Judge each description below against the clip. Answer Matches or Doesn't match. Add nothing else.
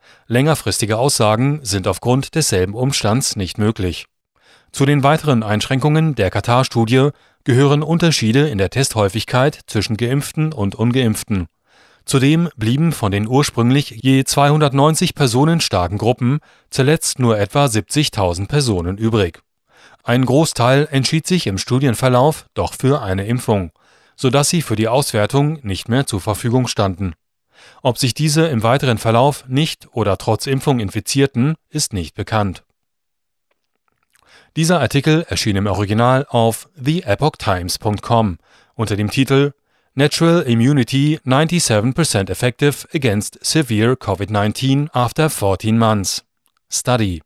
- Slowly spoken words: Matches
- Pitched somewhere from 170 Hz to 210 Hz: Doesn't match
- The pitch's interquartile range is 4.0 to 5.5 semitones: Matches